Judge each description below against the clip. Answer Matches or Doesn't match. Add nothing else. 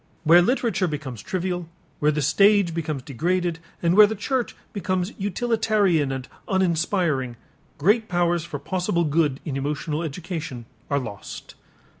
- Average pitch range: Matches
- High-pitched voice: Doesn't match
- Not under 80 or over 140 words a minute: Matches